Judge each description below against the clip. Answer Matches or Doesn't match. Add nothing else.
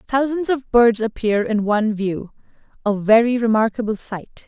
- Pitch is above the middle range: Matches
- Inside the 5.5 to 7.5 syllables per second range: Doesn't match